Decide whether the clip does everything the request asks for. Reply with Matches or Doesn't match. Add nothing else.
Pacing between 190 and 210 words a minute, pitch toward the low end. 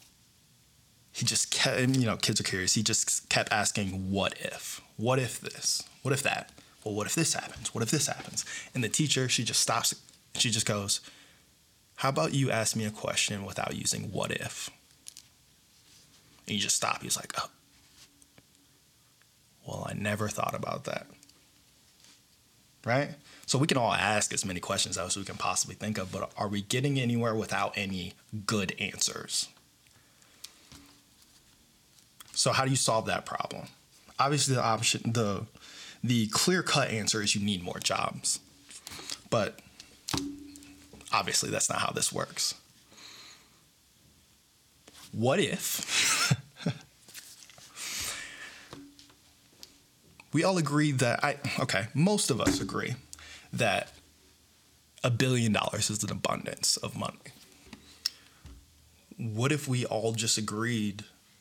Doesn't match